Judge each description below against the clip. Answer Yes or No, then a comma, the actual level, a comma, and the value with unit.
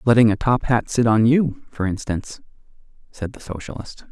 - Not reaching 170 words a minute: No, average, 175 wpm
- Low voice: Yes, low, 115 Hz